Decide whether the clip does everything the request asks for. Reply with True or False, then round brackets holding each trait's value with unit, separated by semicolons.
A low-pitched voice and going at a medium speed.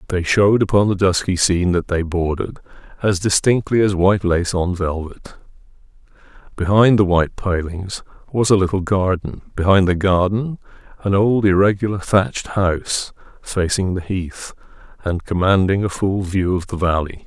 True (95 Hz; 150 wpm)